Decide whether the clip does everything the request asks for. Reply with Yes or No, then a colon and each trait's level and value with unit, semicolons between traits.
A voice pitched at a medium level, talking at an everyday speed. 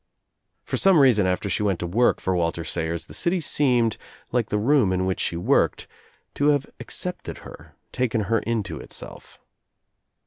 No: low, 105 Hz; average, 170 wpm